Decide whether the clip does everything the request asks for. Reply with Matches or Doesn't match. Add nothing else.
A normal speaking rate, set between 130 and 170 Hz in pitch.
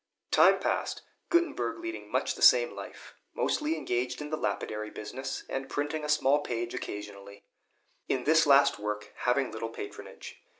Matches